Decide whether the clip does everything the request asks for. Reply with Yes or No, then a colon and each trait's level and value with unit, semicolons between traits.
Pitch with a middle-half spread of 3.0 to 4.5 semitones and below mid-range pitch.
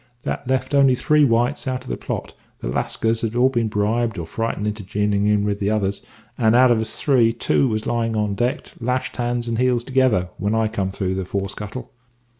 Yes: average, 3.3 semitones; low, 115 Hz